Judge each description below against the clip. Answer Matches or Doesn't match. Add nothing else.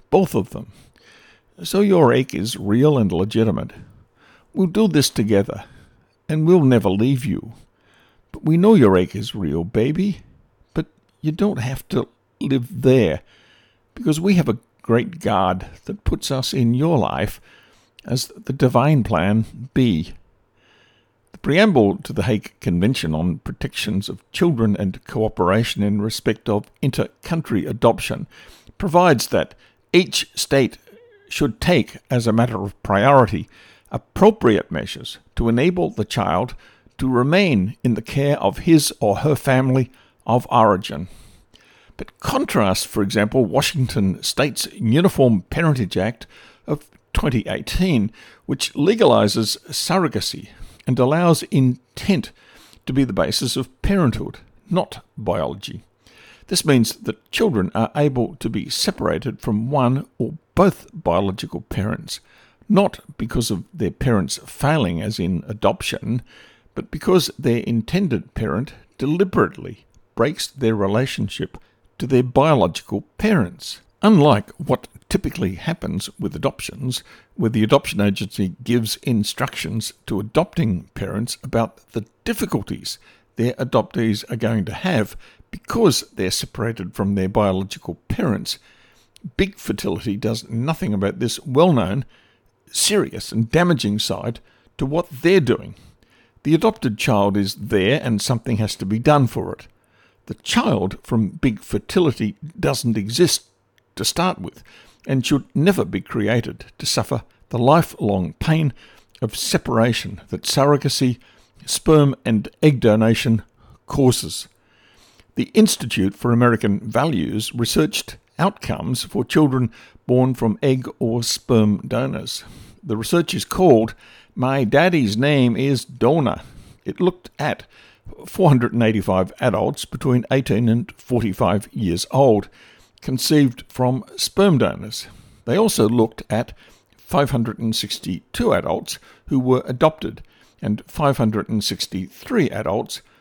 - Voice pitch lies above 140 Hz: Doesn't match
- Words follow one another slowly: Matches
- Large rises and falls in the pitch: Doesn't match